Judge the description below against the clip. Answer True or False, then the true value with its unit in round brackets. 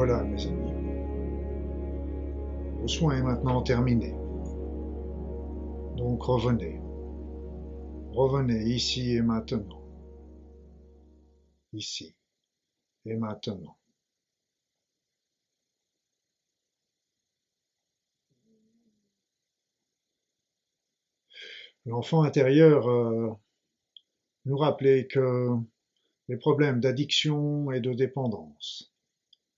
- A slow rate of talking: True (60 wpm)